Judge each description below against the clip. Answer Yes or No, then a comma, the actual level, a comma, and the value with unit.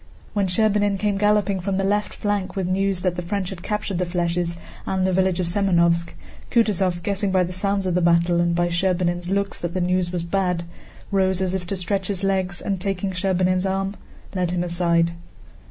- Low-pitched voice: No, medium, 185 Hz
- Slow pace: No, average, 200 wpm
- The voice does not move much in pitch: Yes, narrow, 2.0 semitones